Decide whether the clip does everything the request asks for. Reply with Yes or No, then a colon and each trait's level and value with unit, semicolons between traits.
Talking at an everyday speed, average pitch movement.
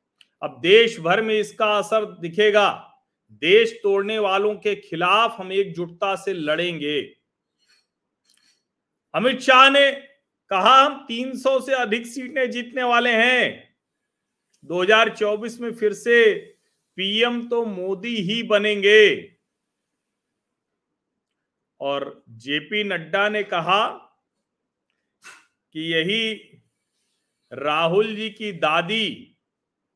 No: slow, 95 wpm; average, 4.2 semitones